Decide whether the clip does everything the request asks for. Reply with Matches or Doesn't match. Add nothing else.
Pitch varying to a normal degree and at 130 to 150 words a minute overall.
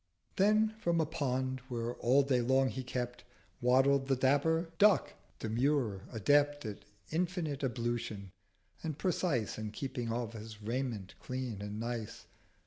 Matches